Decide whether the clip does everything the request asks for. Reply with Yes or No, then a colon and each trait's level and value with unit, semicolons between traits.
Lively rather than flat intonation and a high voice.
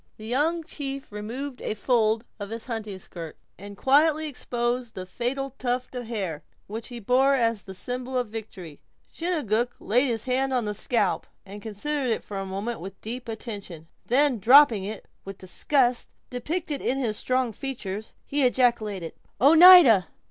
No: average, 4.2 semitones; high, 240 Hz